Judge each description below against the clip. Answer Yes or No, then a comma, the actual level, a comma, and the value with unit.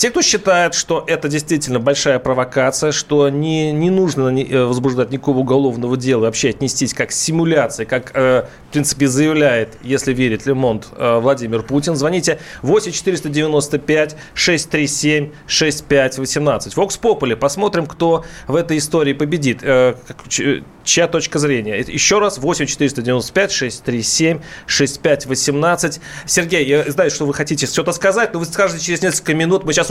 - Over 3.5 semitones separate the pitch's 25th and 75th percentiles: Yes, average, 3.9 semitones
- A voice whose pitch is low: No, medium, 150 Hz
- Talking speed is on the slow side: No, average, 125 wpm